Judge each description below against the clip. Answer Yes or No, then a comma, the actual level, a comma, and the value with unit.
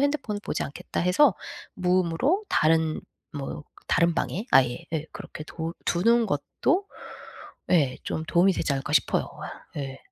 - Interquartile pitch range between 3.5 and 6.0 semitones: Yes, average, 5.2 semitones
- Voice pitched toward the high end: No, medium, 170 Hz